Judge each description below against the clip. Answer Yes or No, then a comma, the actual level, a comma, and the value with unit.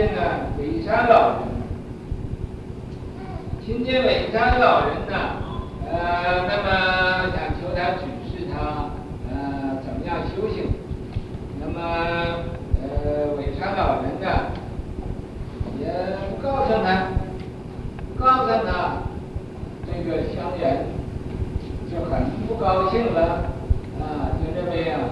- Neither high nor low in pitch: Yes, medium, 170 Hz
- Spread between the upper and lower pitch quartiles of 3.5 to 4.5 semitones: Yes, average, 3.9 semitones